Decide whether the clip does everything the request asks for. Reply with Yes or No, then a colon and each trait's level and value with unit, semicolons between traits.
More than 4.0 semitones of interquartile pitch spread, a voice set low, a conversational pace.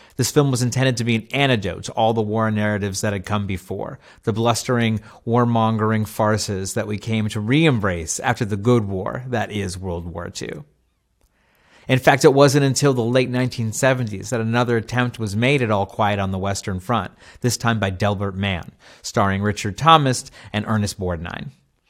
No: average, 3.6 semitones; low, 110 Hz; average, 180 wpm